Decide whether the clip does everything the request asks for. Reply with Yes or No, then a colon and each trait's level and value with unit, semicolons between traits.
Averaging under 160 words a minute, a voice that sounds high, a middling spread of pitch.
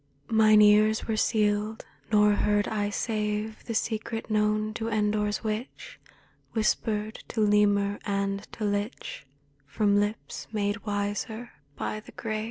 No: slow, 135 wpm; high, 210 Hz; narrow, 1.0 semitones